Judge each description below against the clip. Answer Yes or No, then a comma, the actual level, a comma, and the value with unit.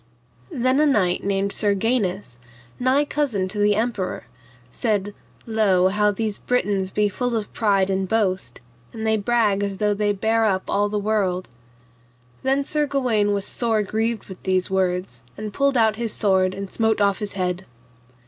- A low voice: No, high, 205 Hz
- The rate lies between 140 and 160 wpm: No, average, 170 wpm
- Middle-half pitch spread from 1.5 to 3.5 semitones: Yes, average, 2.8 semitones